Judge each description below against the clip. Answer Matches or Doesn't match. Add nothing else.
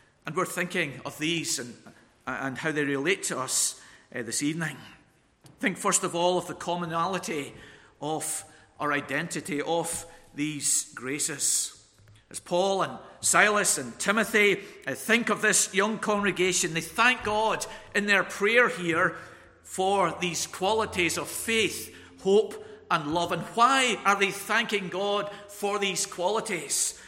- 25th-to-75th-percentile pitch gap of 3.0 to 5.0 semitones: Doesn't match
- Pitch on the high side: Doesn't match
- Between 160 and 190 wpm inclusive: Doesn't match